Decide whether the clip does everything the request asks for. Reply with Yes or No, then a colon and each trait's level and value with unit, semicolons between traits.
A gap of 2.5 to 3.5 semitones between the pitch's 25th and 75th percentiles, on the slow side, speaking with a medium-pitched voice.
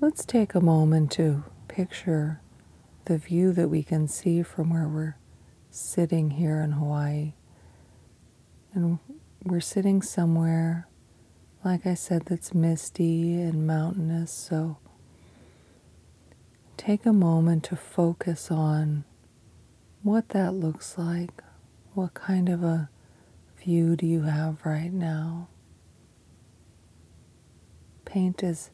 Yes: average, 2.8 semitones; slow, 110 wpm; medium, 165 Hz